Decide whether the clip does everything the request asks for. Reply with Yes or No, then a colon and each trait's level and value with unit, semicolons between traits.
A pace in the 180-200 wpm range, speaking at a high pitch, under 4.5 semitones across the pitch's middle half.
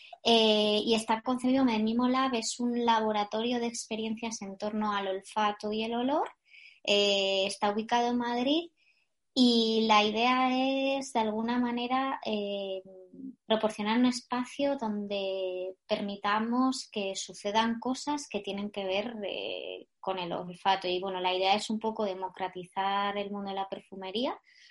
No: average, 145 wpm; high, 220 Hz; average, 3.8 semitones